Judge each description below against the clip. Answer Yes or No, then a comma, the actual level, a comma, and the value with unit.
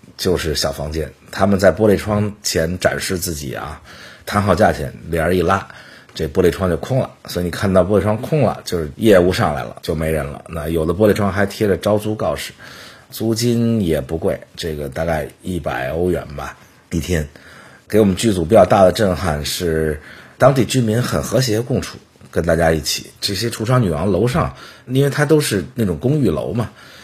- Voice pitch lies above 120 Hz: No, very low, 95 Hz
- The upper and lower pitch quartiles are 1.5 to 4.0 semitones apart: No, average, 5.2 semitones